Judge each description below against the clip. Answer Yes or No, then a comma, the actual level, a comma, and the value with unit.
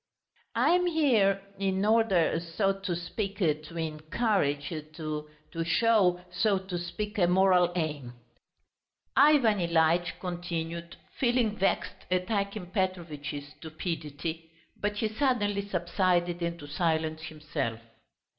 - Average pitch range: Yes, average, 3.9 semitones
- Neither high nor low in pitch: Yes, medium, 175 Hz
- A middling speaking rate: No, slow, 110 wpm